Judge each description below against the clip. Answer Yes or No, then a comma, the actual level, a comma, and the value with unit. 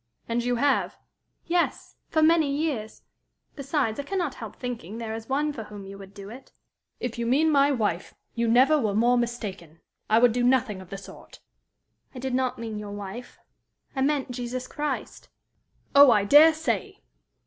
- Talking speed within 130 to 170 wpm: No, average, 180 wpm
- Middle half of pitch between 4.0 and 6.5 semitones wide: Yes, average, 4.5 semitones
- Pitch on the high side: Yes, high, 245 Hz